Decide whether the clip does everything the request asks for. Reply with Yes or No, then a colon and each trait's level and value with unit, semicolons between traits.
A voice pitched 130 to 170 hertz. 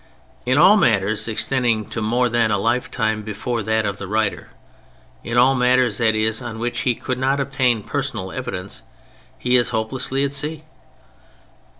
No: low, 120 Hz